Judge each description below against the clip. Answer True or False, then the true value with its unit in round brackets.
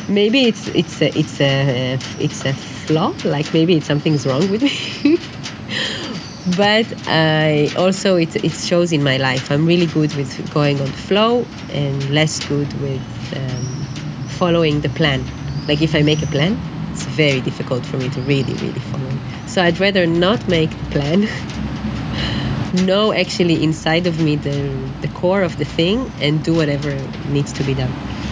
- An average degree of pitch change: True (4.3 semitones)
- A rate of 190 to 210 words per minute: False (170 wpm)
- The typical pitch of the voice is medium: True (155 Hz)